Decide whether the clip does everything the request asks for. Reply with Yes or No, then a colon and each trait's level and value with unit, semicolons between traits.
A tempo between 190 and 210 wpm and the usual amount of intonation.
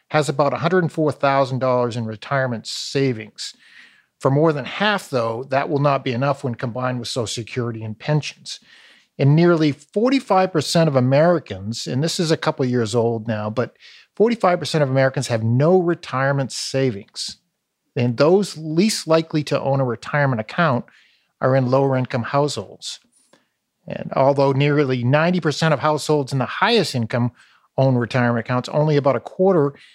No: average, 150 wpm; average, 3.7 semitones